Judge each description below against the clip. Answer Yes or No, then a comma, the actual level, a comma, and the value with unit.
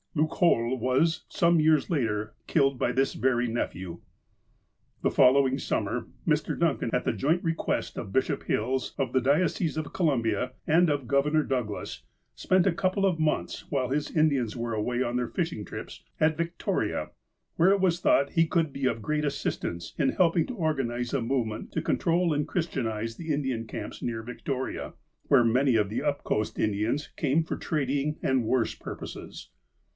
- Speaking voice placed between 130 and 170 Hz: Yes, low, 135 Hz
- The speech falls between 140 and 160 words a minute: No, average, 175 wpm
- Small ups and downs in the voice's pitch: No, average, 4.8 semitones